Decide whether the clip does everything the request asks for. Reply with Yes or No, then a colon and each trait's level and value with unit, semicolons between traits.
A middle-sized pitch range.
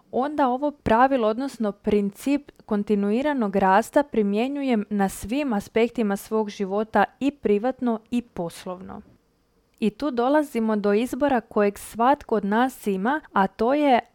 Yes: average, 4.2 semitones